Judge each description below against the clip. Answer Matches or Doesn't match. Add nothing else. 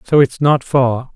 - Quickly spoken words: Matches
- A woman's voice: Doesn't match